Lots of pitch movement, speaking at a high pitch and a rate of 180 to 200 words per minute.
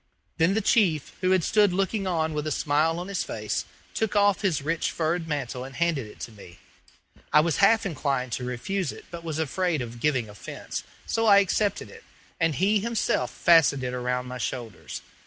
No: wide, 6.7 semitones; medium, 160 Hz; average, 195 wpm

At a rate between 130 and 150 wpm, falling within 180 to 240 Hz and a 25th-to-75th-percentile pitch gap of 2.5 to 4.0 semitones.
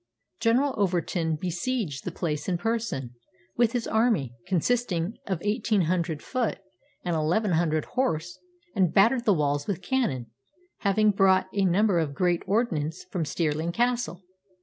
No: average, 145 wpm; medium, 185 Hz; wide, 5.5 semitones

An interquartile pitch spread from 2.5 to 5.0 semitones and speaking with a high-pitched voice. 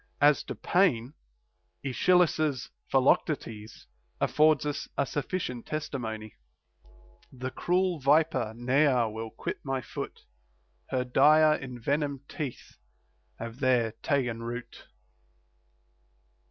No: average, 4.0 semitones; low, 135 Hz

